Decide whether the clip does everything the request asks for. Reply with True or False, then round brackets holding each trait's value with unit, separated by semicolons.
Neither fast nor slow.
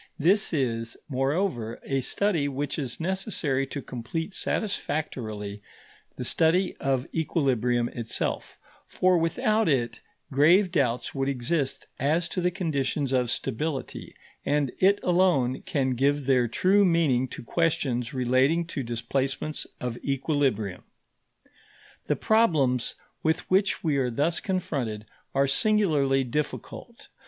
False (120 wpm)